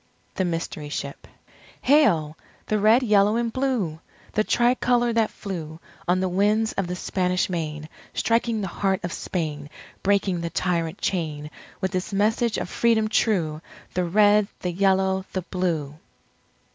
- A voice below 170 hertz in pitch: No, high, 190 Hz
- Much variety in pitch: No, average, 4.2 semitones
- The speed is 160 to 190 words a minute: No, average, 150 wpm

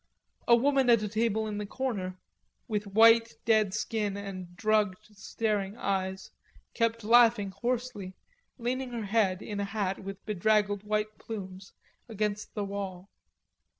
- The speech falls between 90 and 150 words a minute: Yes, average, 140 wpm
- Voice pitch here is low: No, high, 210 Hz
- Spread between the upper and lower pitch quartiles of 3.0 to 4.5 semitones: No, narrow, 2.4 semitones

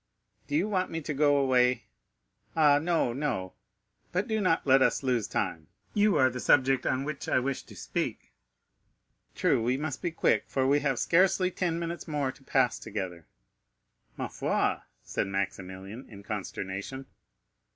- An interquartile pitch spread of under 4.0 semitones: No, wide, 5.5 semitones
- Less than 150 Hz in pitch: Yes, low, 135 Hz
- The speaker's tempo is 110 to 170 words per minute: Yes, average, 160 wpm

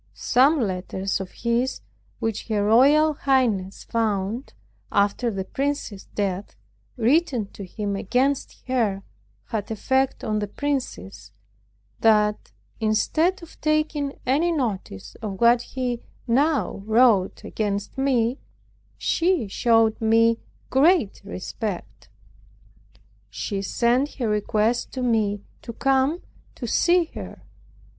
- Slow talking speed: Yes, slow, 110 wpm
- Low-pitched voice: No, high, 230 Hz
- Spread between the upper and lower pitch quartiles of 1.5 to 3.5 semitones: No, average, 4.7 semitones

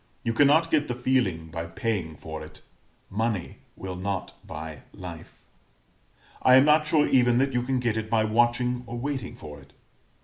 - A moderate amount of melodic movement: No, wide, 6.4 semitones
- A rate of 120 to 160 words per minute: No, average, 175 wpm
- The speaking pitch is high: No, low, 115 Hz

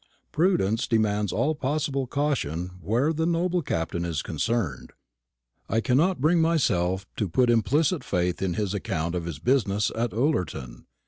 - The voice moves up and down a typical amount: No, wide, 8.6 semitones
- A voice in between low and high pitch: No, low, 115 Hz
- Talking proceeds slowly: No, average, 145 wpm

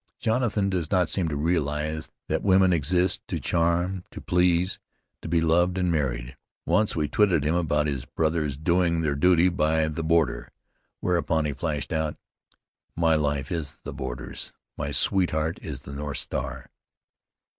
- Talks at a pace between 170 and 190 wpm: No, average, 155 wpm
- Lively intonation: No, average, 3.0 semitones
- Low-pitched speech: Yes, very low, 80 Hz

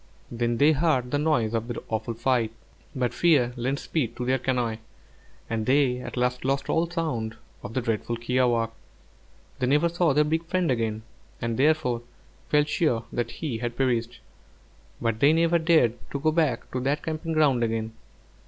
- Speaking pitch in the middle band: No, low, 125 Hz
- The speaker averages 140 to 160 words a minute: No, average, 175 wpm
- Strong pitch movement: No, average, 4.5 semitones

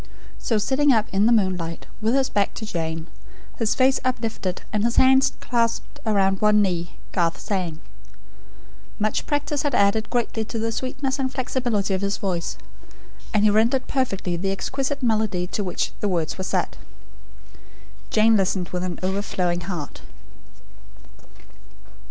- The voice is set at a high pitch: Yes, high, 210 Hz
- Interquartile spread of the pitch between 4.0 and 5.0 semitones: Yes, average, 4.5 semitones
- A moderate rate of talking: Yes, average, 150 wpm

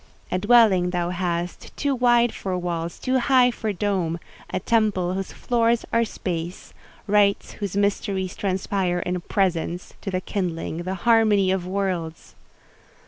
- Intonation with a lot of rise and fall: No, average, 3.3 semitones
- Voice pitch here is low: No, high, 190 Hz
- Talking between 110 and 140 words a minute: Yes, slow, 135 wpm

